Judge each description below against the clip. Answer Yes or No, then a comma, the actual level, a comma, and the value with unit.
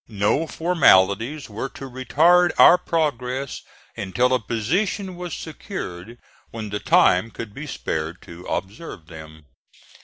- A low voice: Yes, low, 125 Hz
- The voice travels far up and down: Yes, wide, 8.2 semitones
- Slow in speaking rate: Yes, slow, 125 wpm